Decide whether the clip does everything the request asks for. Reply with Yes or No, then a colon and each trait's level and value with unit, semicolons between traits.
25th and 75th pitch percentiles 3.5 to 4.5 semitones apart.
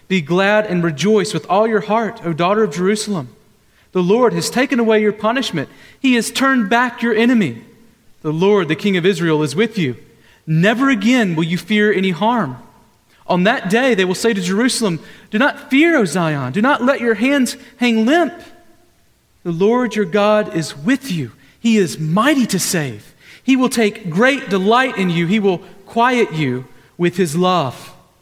No: wide, 5.4 semitones